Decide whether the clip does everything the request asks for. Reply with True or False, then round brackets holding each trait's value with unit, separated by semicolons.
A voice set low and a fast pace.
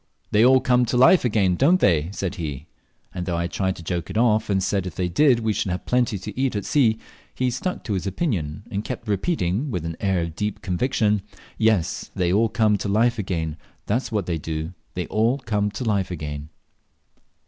True (100 Hz; 215 wpm)